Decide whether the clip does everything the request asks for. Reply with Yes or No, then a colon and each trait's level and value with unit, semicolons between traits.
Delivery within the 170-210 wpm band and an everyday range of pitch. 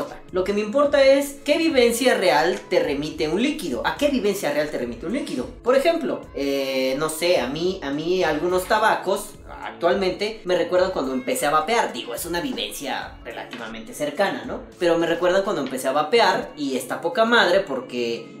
No: average, 185 wpm; wide, 7.8 semitones